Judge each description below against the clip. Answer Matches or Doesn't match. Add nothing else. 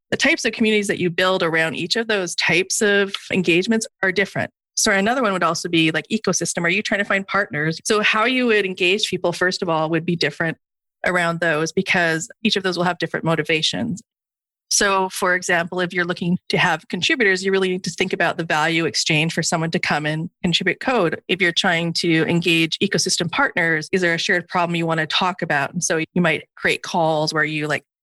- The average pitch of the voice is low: Doesn't match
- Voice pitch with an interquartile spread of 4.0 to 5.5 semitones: Doesn't match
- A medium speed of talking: Doesn't match